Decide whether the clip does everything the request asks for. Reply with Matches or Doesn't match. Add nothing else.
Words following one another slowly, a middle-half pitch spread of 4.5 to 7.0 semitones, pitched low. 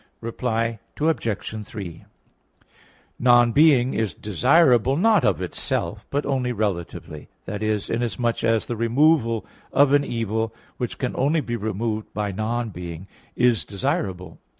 Doesn't match